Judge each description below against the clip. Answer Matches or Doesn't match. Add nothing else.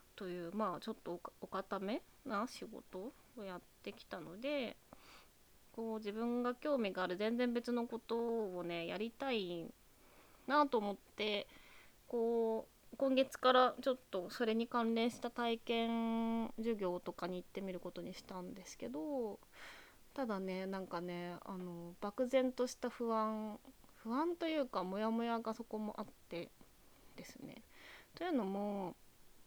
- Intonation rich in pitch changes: Doesn't match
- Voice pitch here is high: Matches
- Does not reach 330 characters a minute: Matches